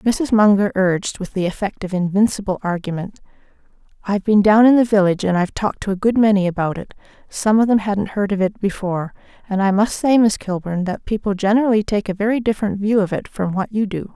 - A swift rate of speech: Yes, fast, 210 wpm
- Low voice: No, high, 200 Hz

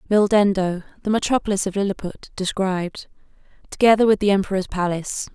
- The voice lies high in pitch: Yes, high, 195 Hz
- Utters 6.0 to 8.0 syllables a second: Yes, 6.1 syllables/s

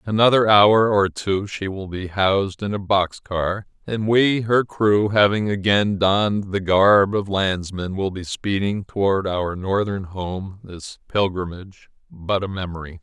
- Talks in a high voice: No, low, 100 Hz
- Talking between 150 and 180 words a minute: Yes, average, 165 wpm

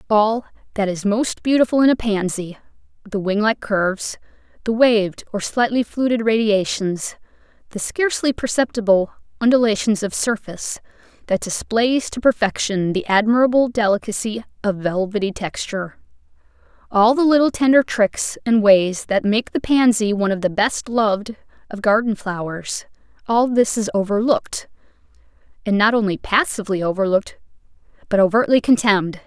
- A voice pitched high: Yes, high, 215 Hz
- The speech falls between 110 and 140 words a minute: Yes, slow, 135 wpm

